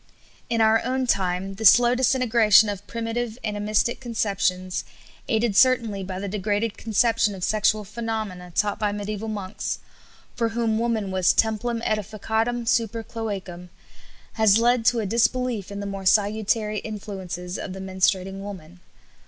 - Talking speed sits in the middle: Yes, average, 145 wpm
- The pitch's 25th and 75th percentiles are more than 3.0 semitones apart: No, average, 2.7 semitones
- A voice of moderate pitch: No, high, 215 Hz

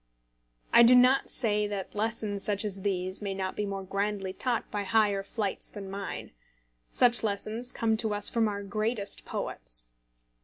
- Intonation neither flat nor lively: No, narrow, 2.1 semitones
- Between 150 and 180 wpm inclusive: Yes, average, 165 wpm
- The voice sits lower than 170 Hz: No, high, 205 Hz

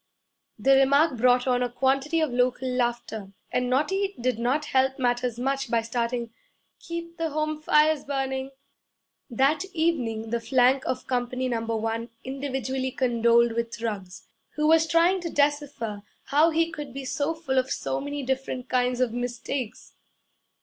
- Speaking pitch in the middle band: No, very high, 260 Hz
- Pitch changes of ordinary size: Yes, average, 3.4 semitones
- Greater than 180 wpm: No, average, 155 wpm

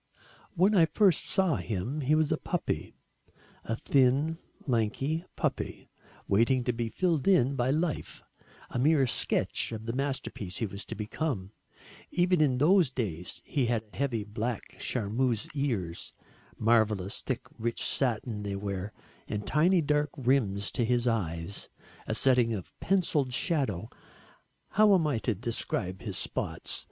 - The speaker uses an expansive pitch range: Yes, wide, 5.7 semitones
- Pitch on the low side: Yes, low, 125 Hz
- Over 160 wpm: No, average, 145 wpm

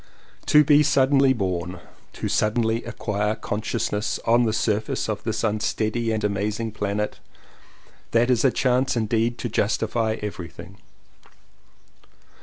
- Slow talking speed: Yes, slow, 120 wpm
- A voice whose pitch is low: Yes, low, 110 Hz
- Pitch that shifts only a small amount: Yes, narrow, 2.3 semitones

